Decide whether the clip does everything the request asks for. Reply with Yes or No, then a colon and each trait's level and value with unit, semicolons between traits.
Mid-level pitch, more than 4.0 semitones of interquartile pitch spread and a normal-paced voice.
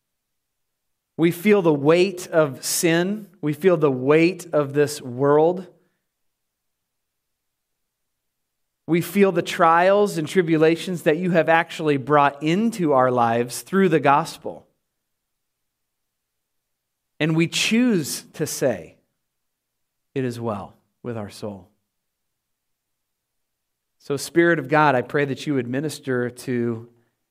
No: medium, 150 Hz; average, 5.0 semitones; slow, 115 wpm